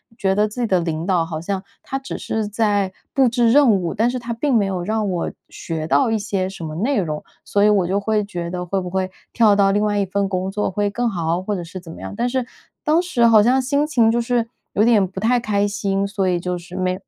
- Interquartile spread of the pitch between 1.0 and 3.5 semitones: No, average, 3.9 semitones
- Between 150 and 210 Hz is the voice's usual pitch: Yes, high, 205 Hz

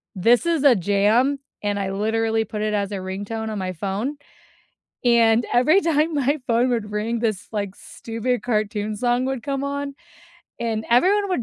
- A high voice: Yes, high, 225 Hz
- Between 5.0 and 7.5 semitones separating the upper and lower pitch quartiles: No, average, 4.1 semitones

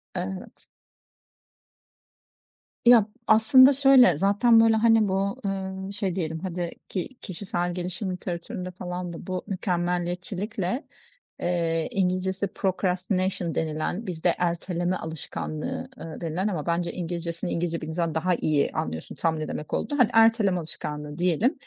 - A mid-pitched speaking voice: Yes, medium, 180 Hz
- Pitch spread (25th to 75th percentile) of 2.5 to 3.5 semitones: Yes, average, 2.8 semitones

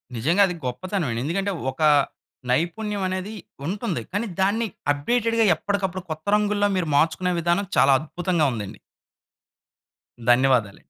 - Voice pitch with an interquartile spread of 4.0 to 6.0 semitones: Yes, average, 5.1 semitones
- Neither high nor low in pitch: Yes, medium, 180 Hz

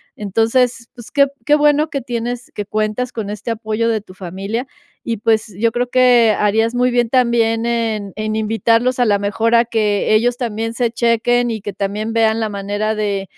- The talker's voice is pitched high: Yes, high, 225 Hz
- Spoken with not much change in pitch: Yes, narrow, 2.2 semitones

